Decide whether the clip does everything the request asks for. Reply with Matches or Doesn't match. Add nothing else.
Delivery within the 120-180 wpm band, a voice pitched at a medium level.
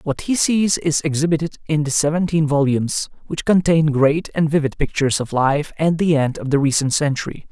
Doesn't match